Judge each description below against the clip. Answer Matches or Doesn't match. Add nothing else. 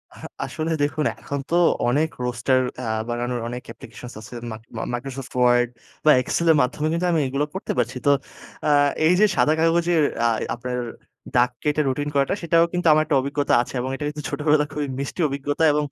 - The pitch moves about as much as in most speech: Matches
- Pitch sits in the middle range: Matches